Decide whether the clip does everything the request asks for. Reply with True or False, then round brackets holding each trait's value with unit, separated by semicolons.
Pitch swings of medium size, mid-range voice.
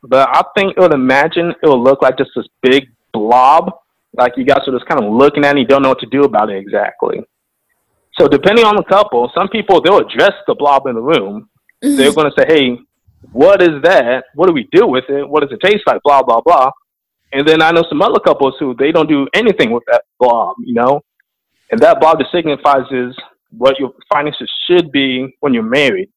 False (6.1 semitones; 145 Hz)